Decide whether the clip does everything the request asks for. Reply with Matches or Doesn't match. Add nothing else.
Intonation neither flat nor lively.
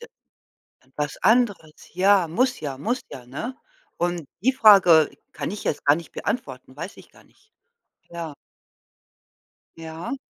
Doesn't match